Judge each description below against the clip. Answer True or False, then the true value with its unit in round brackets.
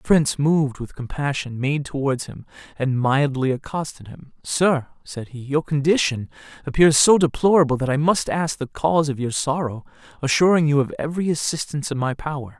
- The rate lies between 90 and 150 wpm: False (175 wpm)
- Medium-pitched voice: True (145 Hz)